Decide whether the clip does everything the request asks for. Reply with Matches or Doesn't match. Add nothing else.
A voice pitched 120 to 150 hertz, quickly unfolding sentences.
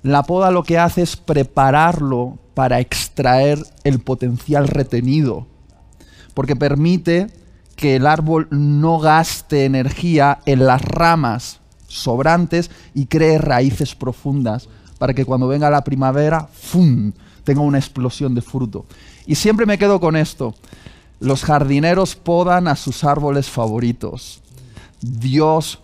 Doesn't match